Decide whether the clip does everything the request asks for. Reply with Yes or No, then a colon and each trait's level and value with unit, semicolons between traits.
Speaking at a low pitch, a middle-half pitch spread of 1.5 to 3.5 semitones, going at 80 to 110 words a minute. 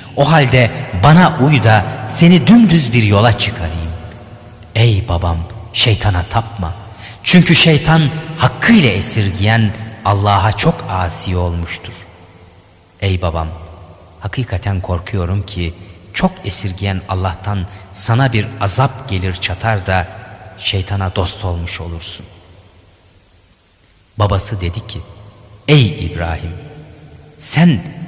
No: low, 100 Hz; average, 4.3 semitones; average, 100 wpm